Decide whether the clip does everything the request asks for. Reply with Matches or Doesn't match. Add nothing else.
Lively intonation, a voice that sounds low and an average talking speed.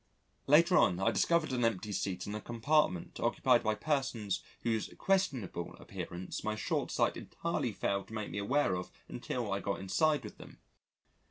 Matches